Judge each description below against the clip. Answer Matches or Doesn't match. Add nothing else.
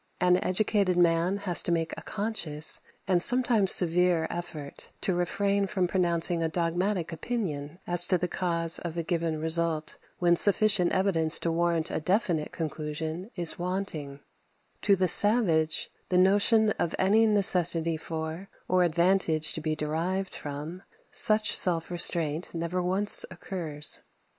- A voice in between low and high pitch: Matches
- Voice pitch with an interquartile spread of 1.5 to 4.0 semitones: Matches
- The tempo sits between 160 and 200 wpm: Doesn't match